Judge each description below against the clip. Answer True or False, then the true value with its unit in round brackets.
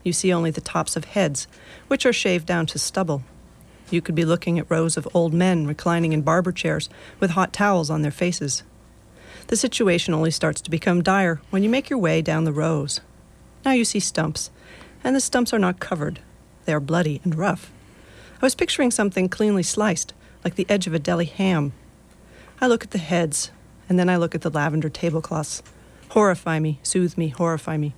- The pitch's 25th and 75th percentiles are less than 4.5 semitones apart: True (3.4 semitones)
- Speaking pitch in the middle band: True (170 Hz)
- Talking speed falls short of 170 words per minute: False (200 wpm)